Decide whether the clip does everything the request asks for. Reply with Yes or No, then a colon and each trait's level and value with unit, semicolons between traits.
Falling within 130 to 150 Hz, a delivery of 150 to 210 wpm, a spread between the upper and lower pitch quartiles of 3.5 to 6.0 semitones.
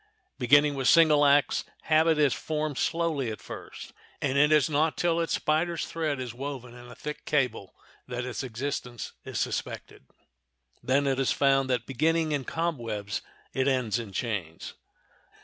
Yes: medium, 140 Hz; average, 160 wpm; average, 3.8 semitones